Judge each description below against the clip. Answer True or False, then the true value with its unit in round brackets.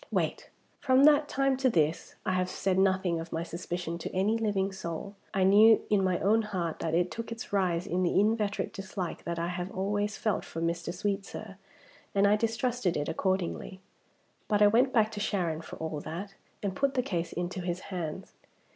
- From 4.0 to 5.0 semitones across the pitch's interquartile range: False (3.4 semitones)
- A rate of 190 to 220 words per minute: True (195 wpm)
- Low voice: False (190 Hz)